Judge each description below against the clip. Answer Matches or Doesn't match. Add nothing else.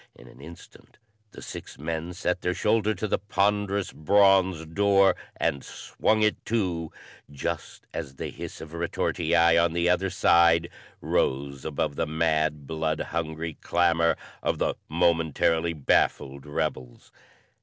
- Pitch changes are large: Doesn't match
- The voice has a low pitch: Matches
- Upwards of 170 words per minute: Doesn't match